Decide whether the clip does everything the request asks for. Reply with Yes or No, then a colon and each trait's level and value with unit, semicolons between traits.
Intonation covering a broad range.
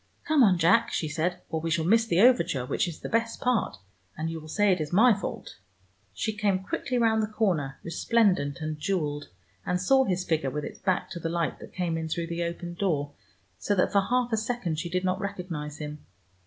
No: average, 4.8 semitones